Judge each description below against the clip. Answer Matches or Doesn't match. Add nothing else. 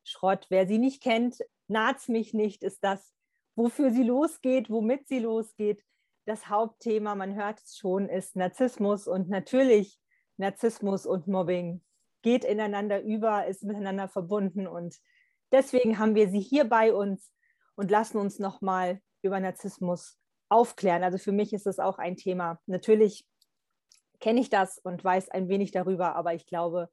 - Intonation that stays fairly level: Doesn't match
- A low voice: Doesn't match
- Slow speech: Doesn't match